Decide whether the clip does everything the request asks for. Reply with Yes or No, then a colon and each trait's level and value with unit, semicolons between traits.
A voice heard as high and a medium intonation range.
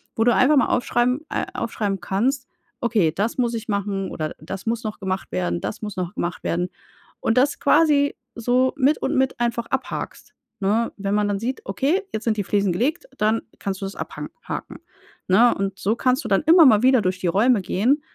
Yes: high, 225 Hz; average, 4.6 semitones